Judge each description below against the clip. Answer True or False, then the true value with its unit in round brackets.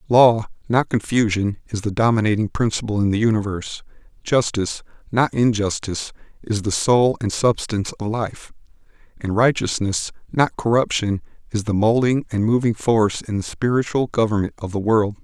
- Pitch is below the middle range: True (110 Hz)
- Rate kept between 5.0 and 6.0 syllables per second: True (5.3 syllables/s)